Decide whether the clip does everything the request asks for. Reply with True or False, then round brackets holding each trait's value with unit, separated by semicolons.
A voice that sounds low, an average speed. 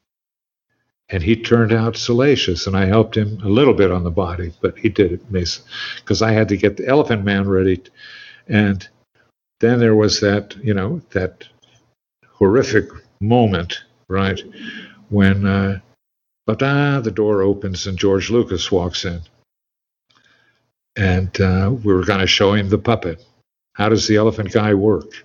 True (100 Hz; 155 wpm)